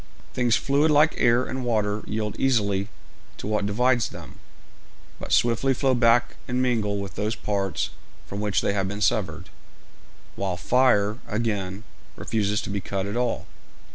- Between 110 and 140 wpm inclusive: No, average, 155 wpm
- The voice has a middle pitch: No, low, 110 Hz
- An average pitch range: Yes, average, 3.3 semitones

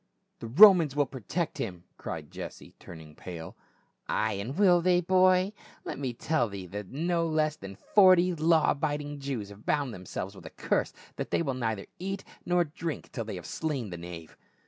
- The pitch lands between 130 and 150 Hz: Yes, medium, 140 Hz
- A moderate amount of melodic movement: No, wide, 8.8 semitones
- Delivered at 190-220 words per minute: Yes, average, 200 wpm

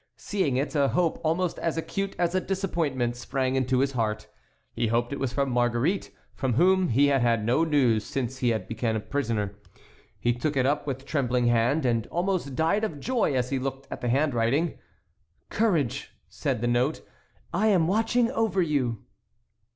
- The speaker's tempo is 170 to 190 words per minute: Yes, average, 180 wpm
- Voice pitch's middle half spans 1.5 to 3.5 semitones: No, wide, 5.6 semitones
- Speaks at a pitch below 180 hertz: Yes, low, 135 Hz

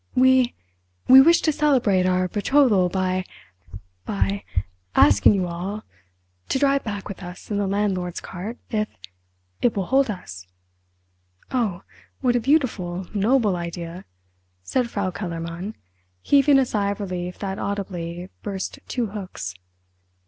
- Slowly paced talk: Yes, slow, 120 wpm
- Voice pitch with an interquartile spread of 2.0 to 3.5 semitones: No, average, 4.8 semitones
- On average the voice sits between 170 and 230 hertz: Yes, high, 190 Hz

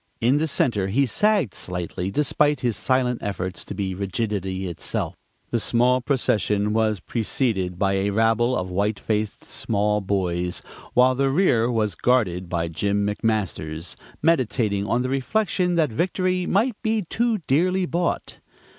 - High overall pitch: No, low, 115 Hz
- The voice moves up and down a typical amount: No, wide, 5.7 semitones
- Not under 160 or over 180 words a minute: No, average, 145 wpm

